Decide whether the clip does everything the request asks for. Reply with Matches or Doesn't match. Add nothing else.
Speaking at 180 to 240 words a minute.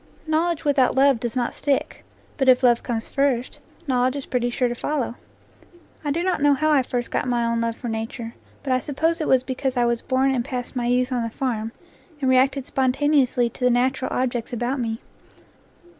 Matches